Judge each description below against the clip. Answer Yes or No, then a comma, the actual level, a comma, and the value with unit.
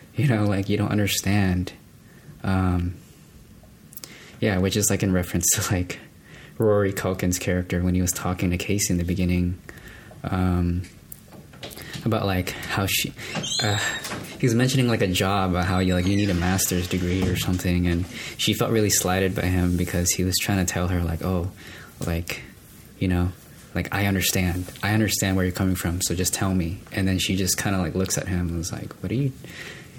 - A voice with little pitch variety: Yes, narrow, 2.2 semitones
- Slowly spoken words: No, average, 195 wpm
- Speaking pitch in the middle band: No, very low, 95 Hz